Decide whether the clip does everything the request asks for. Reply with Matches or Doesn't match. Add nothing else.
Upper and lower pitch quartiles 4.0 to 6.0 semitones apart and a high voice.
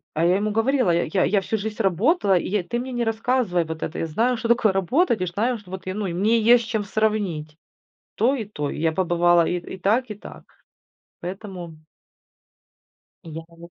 Matches